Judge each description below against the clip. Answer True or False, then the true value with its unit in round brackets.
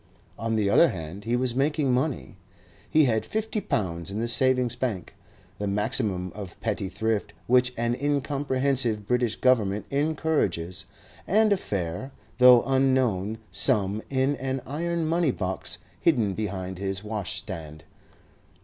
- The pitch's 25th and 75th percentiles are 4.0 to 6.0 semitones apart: True (5.3 semitones)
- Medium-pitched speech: False (120 Hz)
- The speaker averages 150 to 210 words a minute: False (135 wpm)